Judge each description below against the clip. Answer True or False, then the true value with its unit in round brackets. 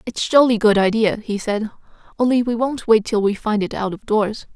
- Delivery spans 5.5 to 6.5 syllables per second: False (5.1 syllables/s)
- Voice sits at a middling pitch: False (220 Hz)